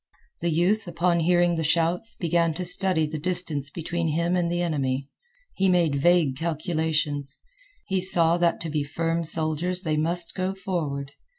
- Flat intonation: Yes, narrow, 2.2 semitones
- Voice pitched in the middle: Yes, medium, 170 Hz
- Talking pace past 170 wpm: No, average, 165 wpm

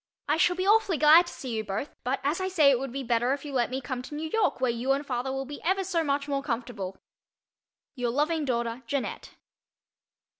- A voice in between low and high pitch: No, very high, 275 Hz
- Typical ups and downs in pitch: Yes, average, 4.1 semitones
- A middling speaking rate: No, fast, 230 wpm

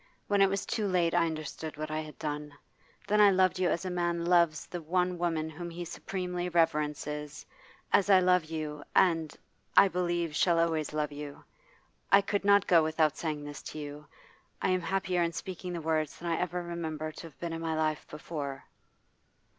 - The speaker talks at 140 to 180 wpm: No, average, 195 wpm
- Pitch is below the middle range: No, medium, 165 Hz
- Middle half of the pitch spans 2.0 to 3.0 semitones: Yes, narrow, 2.6 semitones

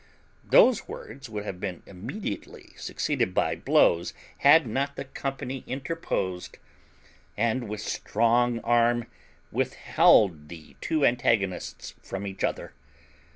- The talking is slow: Yes, slow, 110 wpm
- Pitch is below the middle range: Yes, low, 115 Hz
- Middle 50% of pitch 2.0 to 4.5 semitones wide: No, average, 5.3 semitones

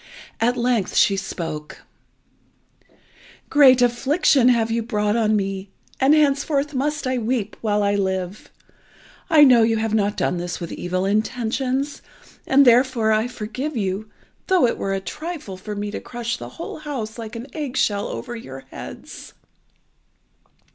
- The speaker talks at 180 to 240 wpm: No, average, 155 wpm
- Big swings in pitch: No, average, 4.3 semitones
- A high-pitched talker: Yes, high, 230 Hz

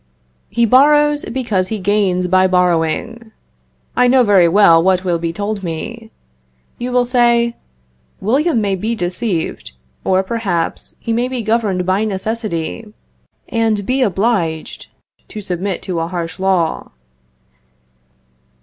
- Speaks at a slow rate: Yes, slow, 130 wpm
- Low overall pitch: No, high, 205 Hz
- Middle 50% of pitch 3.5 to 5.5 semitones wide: Yes, average, 4.4 semitones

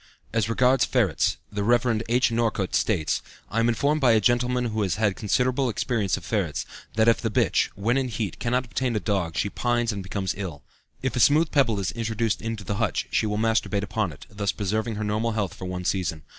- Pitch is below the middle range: Yes, low, 110 Hz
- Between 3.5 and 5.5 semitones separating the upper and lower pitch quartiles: No, average, 3.1 semitones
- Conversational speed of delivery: No, fast, 215 wpm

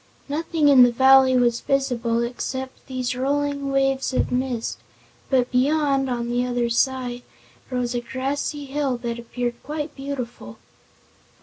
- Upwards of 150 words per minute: No, slow, 135 wpm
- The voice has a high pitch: Yes, very high, 260 Hz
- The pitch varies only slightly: Yes, narrow, 2.1 semitones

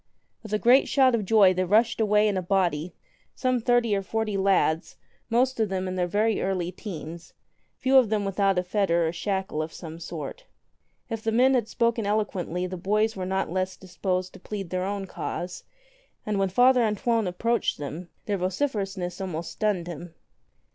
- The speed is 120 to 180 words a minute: No, average, 190 wpm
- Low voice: No, high, 195 Hz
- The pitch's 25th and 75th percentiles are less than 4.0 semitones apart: Yes, average, 3.5 semitones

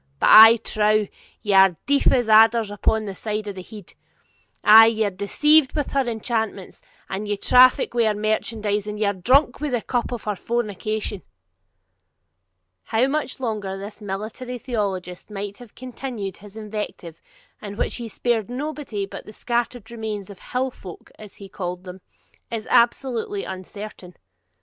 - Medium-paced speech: Yes, average, 165 wpm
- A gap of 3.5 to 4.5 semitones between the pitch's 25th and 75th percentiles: No, average, 2.9 semitones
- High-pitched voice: Yes, high, 215 Hz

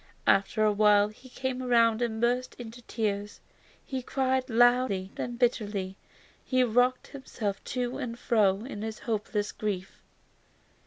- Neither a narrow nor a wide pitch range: Yes, average, 3.2 semitones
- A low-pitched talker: No, high, 230 Hz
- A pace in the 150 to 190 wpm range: No, average, 140 wpm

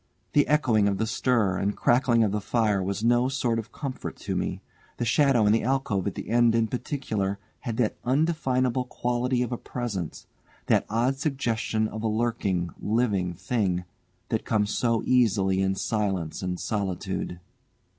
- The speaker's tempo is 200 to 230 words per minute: No, average, 165 wpm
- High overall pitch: No, low, 115 Hz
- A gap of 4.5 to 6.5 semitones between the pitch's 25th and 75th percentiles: No, average, 3.9 semitones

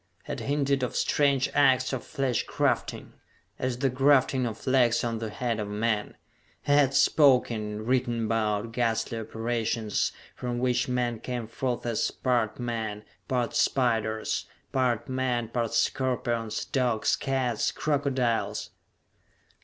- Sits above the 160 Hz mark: No, low, 120 Hz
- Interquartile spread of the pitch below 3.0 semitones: Yes, narrow, 2.4 semitones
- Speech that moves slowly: Yes, slow, 130 wpm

